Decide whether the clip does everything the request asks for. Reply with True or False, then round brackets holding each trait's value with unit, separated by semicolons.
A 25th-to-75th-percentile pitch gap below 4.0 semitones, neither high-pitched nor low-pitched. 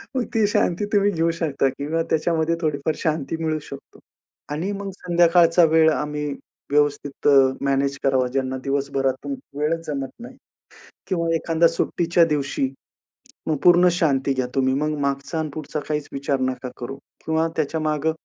True (3.2 semitones; 155 Hz)